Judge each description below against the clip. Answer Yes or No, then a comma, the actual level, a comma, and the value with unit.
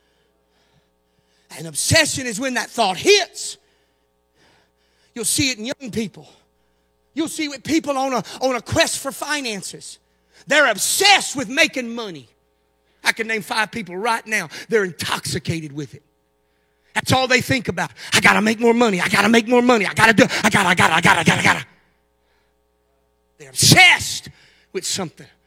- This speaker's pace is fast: No, average, 170 wpm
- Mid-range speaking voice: Yes, medium, 165 Hz